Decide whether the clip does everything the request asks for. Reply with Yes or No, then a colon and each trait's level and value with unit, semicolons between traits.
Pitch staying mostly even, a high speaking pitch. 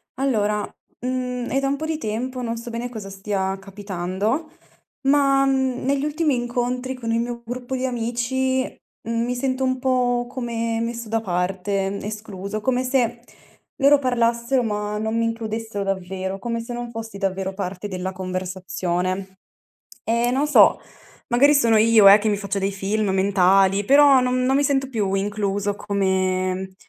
No: average, 4.4 semitones; high, 230 Hz